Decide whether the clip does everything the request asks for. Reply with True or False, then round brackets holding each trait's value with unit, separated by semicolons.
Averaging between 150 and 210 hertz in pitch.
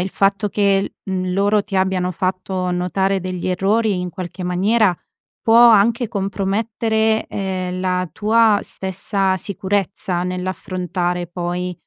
True (190 Hz)